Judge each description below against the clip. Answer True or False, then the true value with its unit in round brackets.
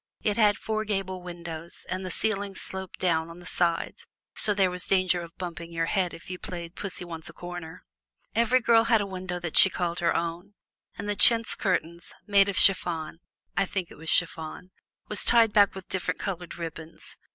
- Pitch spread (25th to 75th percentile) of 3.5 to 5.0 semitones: False (2.9 semitones)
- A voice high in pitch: False (180 Hz)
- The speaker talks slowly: False (195 wpm)